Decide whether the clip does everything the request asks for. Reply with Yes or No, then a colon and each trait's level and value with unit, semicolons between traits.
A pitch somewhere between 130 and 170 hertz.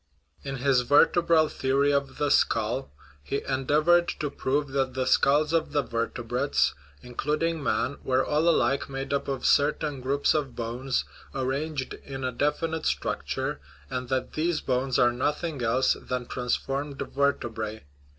Yes: low, 135 Hz